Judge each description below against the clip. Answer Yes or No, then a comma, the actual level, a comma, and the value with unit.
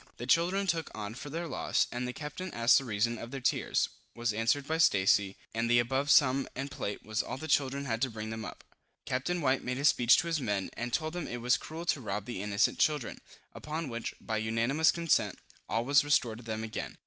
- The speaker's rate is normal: No, fast, 230 wpm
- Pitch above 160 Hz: No, low, 125 Hz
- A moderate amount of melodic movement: Yes, average, 4.6 semitones